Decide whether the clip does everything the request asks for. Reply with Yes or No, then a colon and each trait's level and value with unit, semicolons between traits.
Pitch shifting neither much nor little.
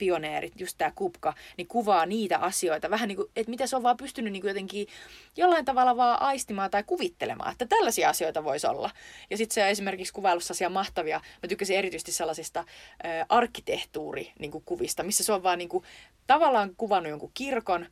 No: wide, 5.8 semitones